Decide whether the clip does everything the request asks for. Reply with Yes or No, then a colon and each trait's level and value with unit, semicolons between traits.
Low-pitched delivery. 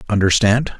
Yes: low, 105 Hz